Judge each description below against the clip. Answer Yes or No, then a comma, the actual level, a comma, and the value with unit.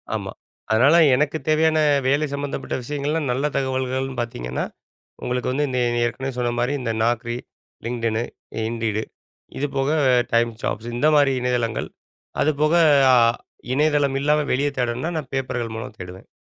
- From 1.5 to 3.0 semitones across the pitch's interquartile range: No, average, 3.5 semitones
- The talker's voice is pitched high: No, low, 130 Hz